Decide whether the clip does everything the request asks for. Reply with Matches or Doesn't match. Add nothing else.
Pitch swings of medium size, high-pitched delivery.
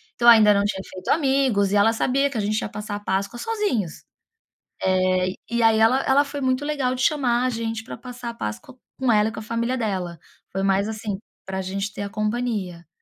Matches